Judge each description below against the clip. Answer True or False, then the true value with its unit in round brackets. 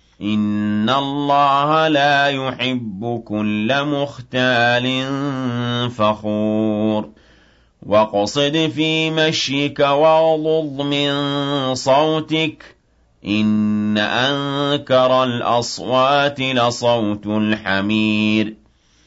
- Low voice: True (125 Hz)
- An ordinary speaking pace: False (55 wpm)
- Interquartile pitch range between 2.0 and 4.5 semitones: False (4.9 semitones)